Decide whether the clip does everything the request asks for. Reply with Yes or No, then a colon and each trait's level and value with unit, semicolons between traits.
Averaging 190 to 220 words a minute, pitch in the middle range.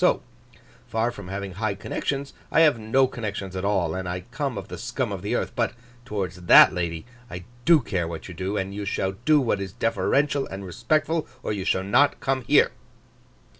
No: fast, 205 wpm; low, 100 Hz